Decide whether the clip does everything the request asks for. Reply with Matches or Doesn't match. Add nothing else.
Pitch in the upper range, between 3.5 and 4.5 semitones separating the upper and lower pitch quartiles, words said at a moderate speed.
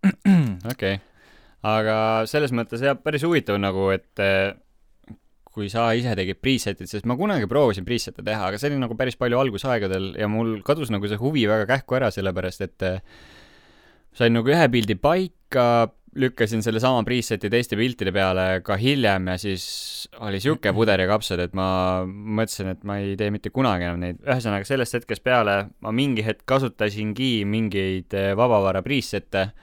Doesn't match